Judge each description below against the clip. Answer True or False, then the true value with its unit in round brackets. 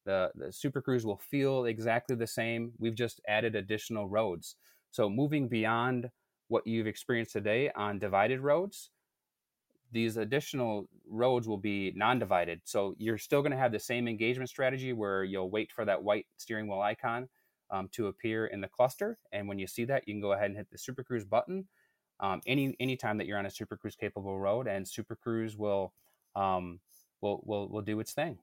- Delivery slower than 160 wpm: False (195 wpm)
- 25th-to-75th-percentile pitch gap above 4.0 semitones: False (3.6 semitones)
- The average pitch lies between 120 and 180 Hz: False (110 Hz)